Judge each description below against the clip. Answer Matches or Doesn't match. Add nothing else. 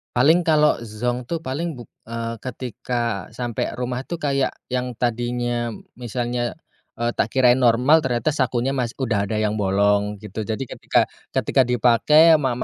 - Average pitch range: Doesn't match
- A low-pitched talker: Matches